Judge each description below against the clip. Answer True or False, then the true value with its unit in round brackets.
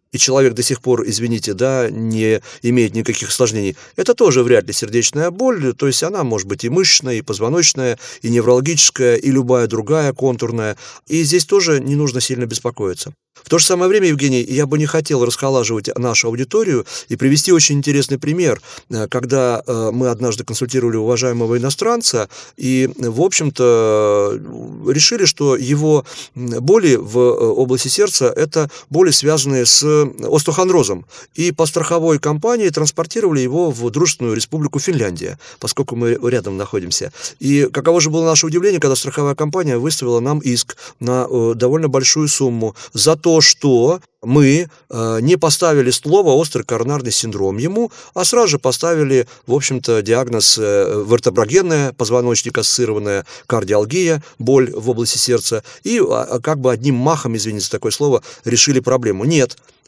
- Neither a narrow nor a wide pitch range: True (4.5 semitones)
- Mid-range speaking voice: False (130 Hz)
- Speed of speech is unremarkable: True (150 wpm)